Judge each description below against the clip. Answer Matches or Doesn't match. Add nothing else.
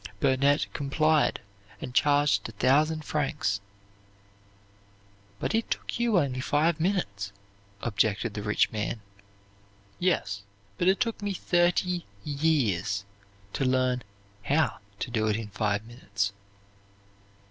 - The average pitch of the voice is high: Doesn't match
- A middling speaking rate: Doesn't match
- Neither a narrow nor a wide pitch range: Doesn't match